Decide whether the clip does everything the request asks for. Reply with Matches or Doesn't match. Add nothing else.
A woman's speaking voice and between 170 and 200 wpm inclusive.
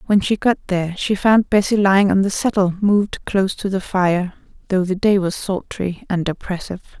Matches